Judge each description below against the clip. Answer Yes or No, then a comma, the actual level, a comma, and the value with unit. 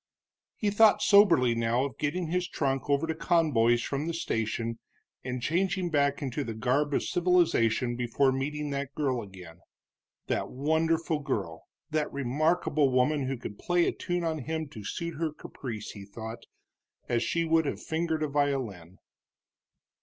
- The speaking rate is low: No, average, 160 wpm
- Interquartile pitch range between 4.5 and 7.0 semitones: Yes, average, 5.2 semitones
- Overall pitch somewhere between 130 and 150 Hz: Yes, medium, 140 Hz